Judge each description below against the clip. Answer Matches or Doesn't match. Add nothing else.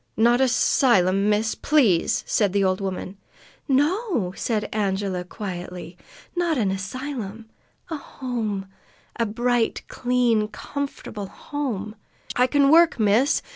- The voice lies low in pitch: Doesn't match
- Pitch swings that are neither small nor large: Matches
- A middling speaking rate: Doesn't match